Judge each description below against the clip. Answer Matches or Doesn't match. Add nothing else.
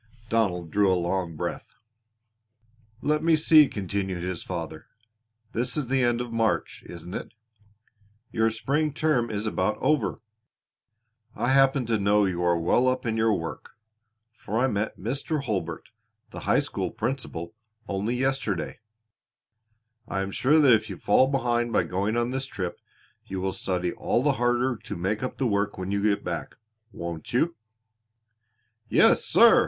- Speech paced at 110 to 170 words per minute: Matches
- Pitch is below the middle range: Matches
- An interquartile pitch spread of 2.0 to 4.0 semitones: Doesn't match